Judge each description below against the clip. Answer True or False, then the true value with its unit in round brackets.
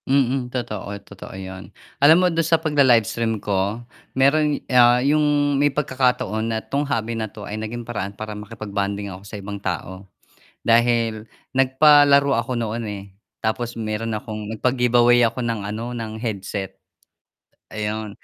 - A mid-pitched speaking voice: False (115 Hz)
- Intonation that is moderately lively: True (3.3 semitones)